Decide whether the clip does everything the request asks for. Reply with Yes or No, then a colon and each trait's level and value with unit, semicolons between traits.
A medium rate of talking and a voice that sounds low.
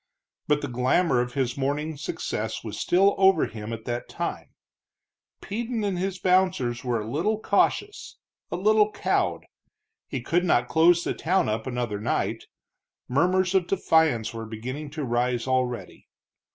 No: average, 150 wpm; medium, 145 Hz